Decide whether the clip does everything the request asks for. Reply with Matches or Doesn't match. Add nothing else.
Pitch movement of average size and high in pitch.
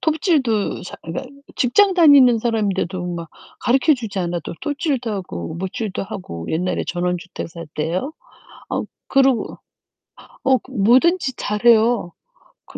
Doesn't match